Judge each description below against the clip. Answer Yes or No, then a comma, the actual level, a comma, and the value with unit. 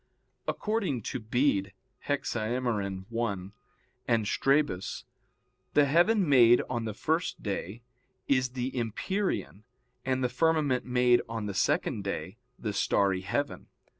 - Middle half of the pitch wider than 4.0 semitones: Yes, average, 5.2 semitones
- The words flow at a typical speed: No, slow, 120 wpm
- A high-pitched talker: No, low, 120 Hz